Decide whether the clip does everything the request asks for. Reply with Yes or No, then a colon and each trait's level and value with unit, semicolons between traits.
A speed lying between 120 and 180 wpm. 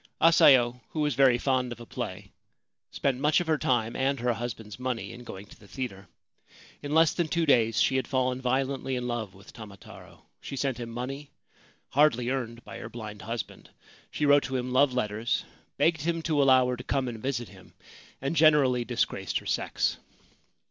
No: average, 190 wpm